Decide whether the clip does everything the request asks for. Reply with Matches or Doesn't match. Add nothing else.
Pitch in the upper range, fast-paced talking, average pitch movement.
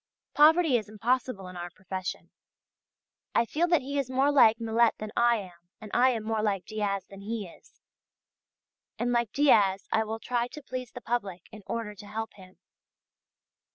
Doesn't match